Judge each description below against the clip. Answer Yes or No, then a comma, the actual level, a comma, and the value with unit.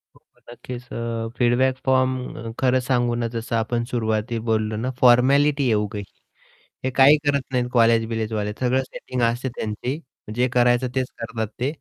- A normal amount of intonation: No, narrow, 2.2 semitones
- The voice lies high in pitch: No, low, 120 Hz